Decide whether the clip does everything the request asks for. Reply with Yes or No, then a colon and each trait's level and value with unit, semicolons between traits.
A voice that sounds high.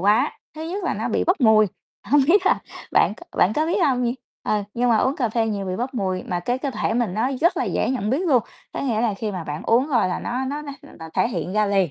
Yes: high, 235 Hz